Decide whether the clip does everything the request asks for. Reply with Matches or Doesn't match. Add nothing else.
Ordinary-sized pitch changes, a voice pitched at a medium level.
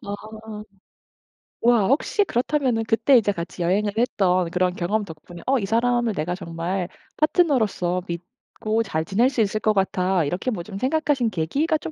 Doesn't match